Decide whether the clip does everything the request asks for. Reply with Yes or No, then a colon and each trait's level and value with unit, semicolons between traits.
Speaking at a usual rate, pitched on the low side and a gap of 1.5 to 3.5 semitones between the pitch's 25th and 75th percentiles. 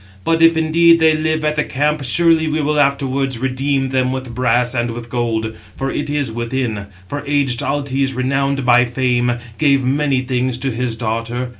Yes: average, 180 wpm; low, 130 Hz; average, 3.0 semitones